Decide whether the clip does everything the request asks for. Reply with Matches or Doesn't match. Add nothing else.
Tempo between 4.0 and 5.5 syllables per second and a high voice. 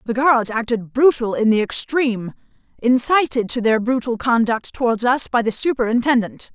Matches